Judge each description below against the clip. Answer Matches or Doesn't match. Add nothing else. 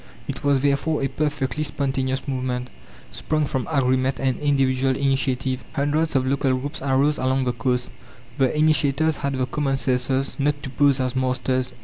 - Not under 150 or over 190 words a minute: Matches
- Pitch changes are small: Matches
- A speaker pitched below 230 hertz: Matches